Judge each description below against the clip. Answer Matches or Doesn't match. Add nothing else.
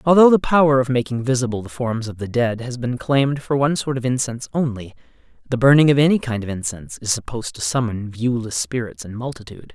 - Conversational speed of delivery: Doesn't match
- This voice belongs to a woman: Doesn't match